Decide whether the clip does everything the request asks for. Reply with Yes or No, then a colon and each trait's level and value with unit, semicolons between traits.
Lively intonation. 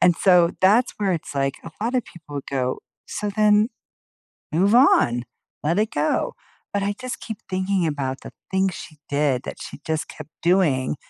Yes: wide, 5.8 semitones